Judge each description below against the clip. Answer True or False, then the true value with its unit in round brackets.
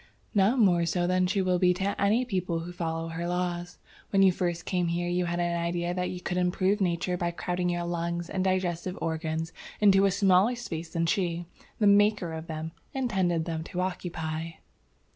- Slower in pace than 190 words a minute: False (195 wpm)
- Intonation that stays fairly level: True (1.8 semitones)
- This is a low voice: False (175 Hz)